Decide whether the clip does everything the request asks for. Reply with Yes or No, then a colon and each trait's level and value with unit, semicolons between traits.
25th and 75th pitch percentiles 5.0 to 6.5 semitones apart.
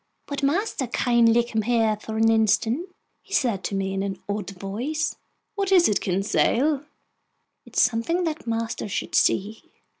Yes: wide, 5.5 semitones